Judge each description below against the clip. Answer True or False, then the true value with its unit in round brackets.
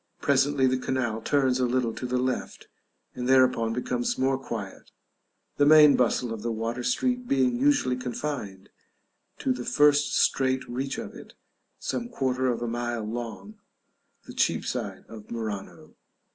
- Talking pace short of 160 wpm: True (150 wpm)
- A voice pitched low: True (125 Hz)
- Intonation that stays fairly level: True (2.2 semitones)